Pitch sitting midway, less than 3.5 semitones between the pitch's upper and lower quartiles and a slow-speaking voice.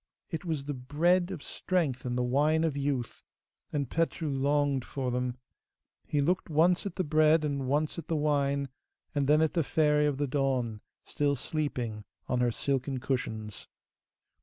No: medium, 145 Hz; average, 3.1 semitones; average, 170 wpm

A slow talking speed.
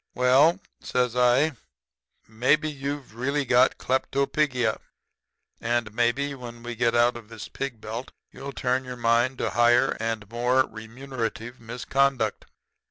Yes: slow, 130 wpm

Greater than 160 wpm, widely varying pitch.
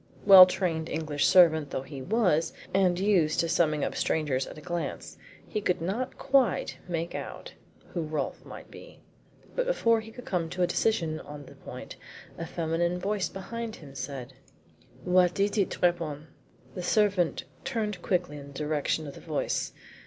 No: average, 170 wpm; average, 4.3 semitones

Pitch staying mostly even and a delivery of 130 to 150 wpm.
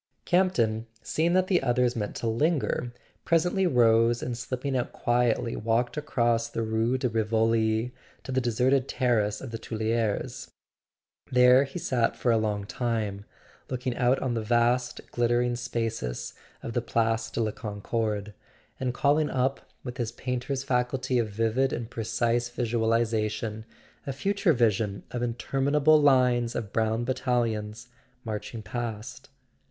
Yes: narrow, 2.3 semitones; average, 145 wpm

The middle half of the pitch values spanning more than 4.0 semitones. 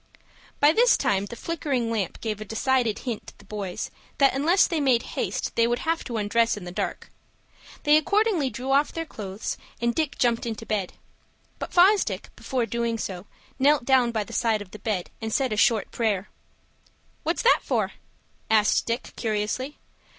Yes: average, 4.8 semitones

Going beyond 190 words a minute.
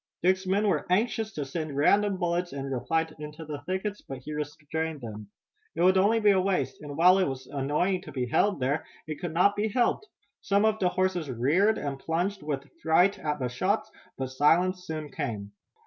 Yes: average, 200 wpm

